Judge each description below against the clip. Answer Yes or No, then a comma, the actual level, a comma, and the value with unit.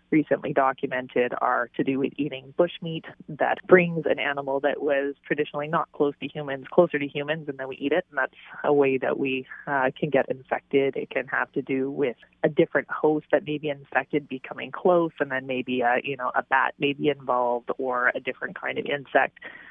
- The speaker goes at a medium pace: No, fast, 210 wpm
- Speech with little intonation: Yes, narrow, 2.1 semitones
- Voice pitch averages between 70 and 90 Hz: No, medium, 140 Hz